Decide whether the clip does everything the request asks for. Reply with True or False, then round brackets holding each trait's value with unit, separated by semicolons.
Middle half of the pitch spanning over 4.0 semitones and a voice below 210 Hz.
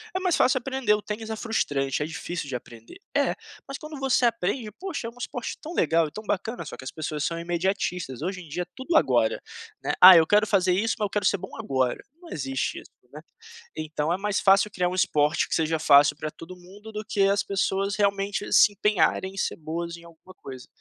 True (4.7 semitones; 190 Hz)